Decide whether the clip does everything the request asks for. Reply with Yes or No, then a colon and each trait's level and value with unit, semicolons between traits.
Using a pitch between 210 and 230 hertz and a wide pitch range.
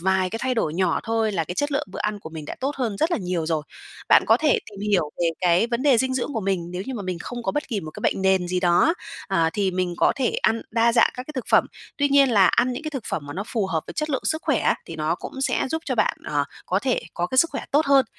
Yes: high, 215 Hz; wide, 6.7 semitones